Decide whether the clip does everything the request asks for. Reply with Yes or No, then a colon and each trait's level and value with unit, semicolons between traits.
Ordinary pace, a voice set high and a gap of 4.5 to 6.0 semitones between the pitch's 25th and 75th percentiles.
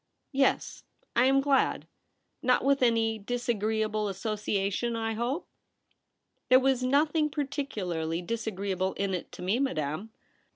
Yes: average, 155 wpm; high, 225 Hz; average, 5.1 semitones